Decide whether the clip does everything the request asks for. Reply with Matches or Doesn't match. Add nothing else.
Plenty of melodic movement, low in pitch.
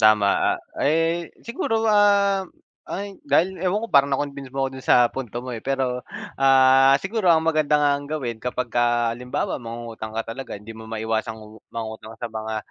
Matches